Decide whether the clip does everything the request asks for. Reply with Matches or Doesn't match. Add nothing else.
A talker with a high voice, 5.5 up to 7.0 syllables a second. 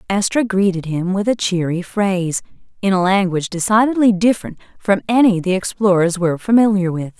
Matches